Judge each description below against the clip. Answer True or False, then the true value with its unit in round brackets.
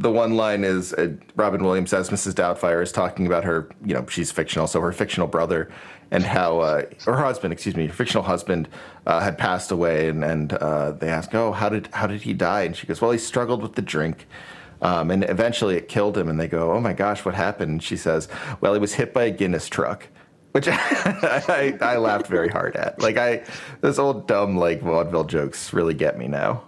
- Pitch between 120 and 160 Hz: False (95 Hz)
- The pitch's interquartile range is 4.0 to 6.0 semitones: True (4.9 semitones)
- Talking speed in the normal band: False (225 wpm)